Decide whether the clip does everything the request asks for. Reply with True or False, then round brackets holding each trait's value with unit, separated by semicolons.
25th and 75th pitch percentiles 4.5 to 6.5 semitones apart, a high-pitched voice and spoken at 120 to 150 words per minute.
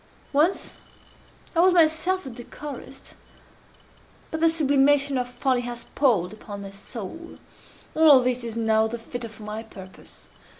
True (5.1 semitones; 250 Hz; 140 wpm)